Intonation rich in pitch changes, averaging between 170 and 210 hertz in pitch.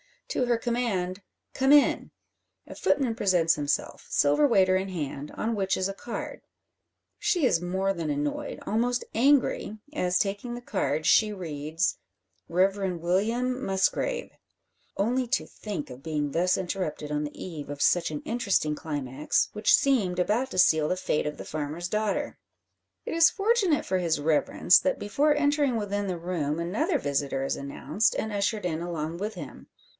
Yes: wide, 6.8 semitones; high, 190 Hz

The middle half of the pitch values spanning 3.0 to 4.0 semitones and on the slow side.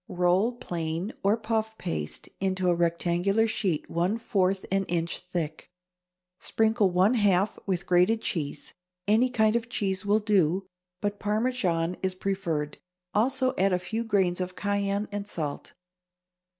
No: average, 3.5 semitones; average, 145 wpm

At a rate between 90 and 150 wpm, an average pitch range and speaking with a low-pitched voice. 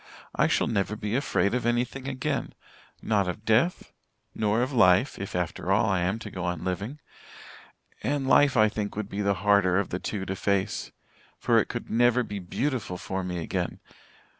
No: average, 190 wpm; average, 4.0 semitones; low, 105 Hz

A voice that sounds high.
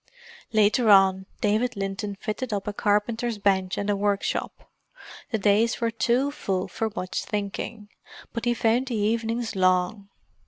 Yes: high, 210 Hz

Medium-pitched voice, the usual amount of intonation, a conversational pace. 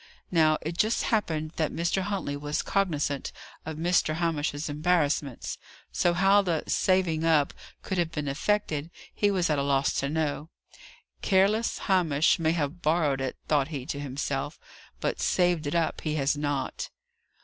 Yes: medium, 160 Hz; average, 3.4 semitones; average, 160 wpm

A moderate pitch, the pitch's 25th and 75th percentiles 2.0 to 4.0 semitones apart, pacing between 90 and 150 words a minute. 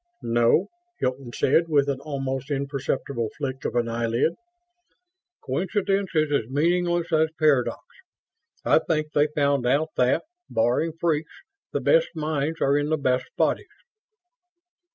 Yes: medium, 145 Hz; average, 3.4 semitones; slow, 135 wpm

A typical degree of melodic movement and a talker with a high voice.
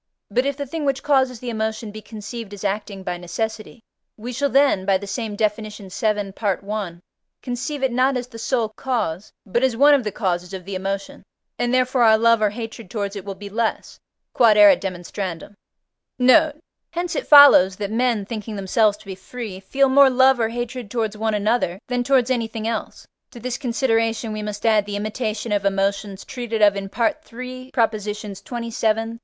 Yes: average, 3.5 semitones; high, 220 Hz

